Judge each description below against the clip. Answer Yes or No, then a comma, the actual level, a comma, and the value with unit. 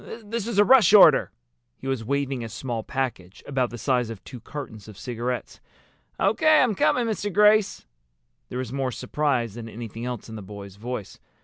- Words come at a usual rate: Yes, average, 185 wpm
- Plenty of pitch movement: Yes, wide, 7.2 semitones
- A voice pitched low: Yes, low, 125 Hz